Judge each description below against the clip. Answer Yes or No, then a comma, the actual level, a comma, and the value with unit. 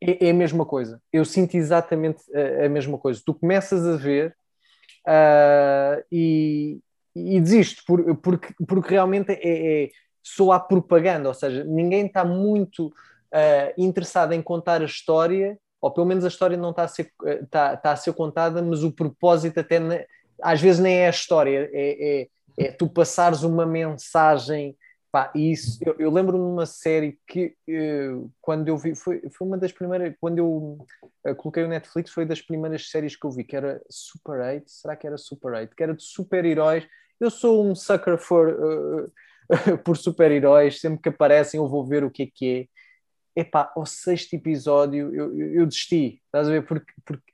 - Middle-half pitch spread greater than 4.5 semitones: No, average, 2.8 semitones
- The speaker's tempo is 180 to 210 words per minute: Yes, fast, 185 wpm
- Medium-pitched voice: Yes, medium, 160 Hz